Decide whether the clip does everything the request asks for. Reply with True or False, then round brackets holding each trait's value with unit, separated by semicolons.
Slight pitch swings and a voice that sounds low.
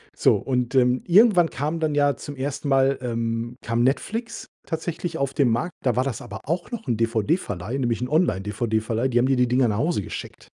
False (4.7 semitones; 130 Hz)